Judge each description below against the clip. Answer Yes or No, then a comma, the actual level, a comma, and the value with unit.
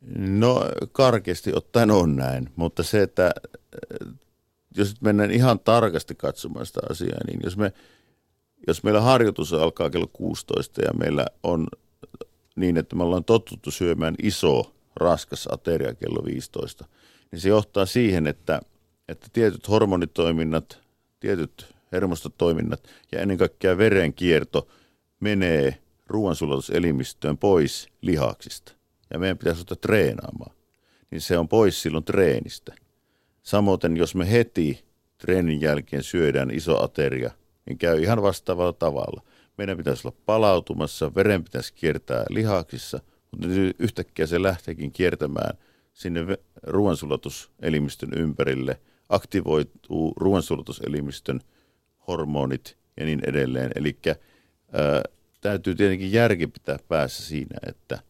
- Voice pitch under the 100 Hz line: Yes, very low, 90 Hz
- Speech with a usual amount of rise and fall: Yes, average, 4.4 semitones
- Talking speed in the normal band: Yes, average, 115 wpm